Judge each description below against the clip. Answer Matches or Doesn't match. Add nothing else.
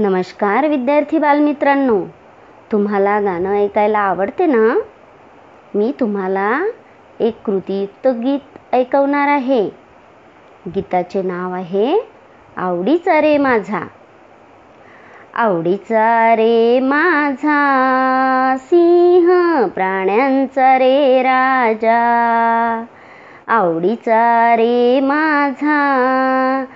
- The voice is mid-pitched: Doesn't match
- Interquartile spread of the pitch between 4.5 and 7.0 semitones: Matches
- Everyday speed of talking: Doesn't match